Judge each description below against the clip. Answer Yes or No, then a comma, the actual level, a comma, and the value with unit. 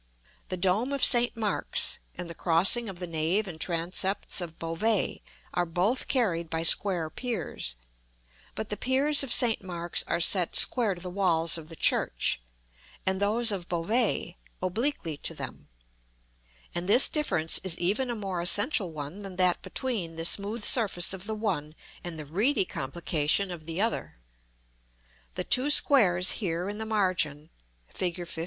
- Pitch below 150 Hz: No, medium, 185 Hz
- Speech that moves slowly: No, average, 160 wpm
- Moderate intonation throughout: Yes, average, 4.5 semitones